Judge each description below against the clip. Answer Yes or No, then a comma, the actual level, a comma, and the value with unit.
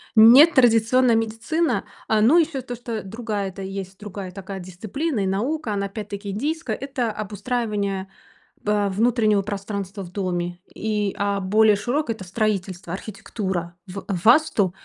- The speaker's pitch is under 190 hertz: No, high, 210 Hz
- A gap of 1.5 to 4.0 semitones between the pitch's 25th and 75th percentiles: Yes, average, 3.1 semitones